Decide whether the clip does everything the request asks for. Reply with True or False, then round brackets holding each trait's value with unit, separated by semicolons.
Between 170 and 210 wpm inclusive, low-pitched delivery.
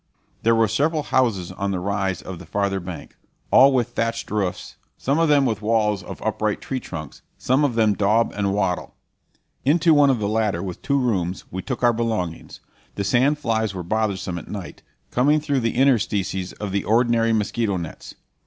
True (190 wpm; 110 Hz)